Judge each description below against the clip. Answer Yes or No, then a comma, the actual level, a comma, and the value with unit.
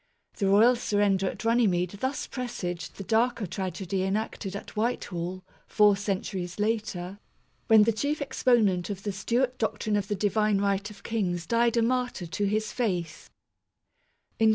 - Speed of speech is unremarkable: Yes, average, 150 wpm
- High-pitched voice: Yes, high, 205 Hz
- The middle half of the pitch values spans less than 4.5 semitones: Yes, average, 3.2 semitones